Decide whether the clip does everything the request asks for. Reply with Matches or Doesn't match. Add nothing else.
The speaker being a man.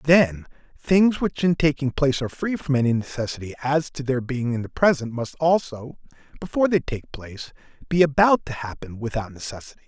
Matches